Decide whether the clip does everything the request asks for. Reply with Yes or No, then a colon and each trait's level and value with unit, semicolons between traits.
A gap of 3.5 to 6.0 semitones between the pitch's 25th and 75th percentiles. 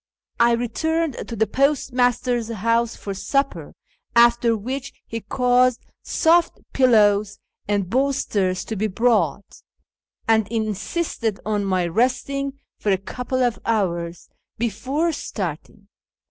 Yes: average, 3.8 semitones